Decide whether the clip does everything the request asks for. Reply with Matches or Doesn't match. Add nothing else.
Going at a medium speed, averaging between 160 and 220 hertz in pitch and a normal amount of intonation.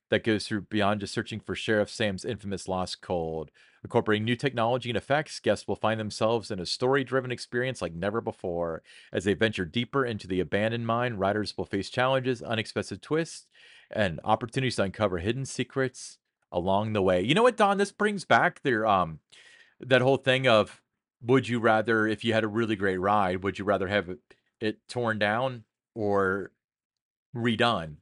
Doesn't match